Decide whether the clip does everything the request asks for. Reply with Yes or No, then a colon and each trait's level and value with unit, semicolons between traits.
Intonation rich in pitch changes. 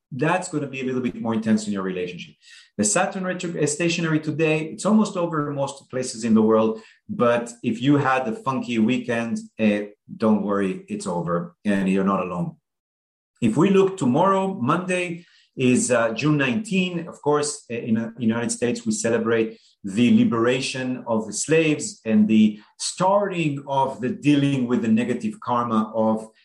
Yes: wide, 6.1 semitones